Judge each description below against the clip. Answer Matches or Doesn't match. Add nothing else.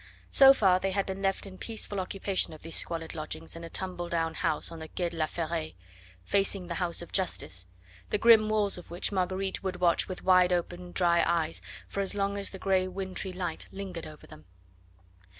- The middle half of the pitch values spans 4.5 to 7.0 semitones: Doesn't match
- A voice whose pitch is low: Doesn't match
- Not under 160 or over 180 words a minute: Doesn't match